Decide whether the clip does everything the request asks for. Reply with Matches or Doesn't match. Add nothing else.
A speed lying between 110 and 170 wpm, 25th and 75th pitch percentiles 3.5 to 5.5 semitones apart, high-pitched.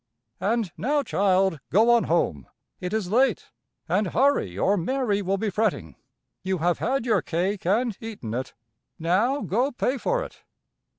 Matches